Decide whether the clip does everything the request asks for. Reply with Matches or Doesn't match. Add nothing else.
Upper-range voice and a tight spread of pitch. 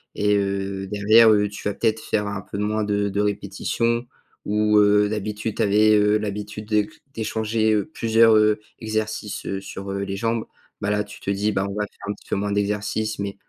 Doesn't match